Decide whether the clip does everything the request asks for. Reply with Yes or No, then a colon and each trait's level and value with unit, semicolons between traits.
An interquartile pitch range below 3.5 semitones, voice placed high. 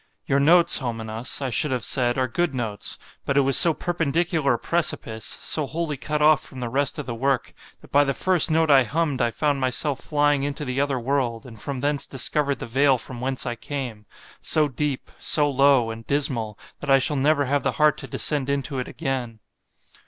No: average, 2.8 semitones; medium, 140 Hz